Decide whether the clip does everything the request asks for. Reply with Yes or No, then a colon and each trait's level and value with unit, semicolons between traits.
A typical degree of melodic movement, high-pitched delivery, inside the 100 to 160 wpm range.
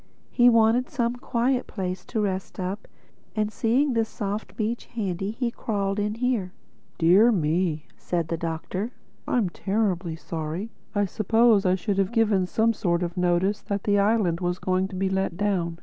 No: average, 3.7 semitones; high, 200 Hz; average, 170 wpm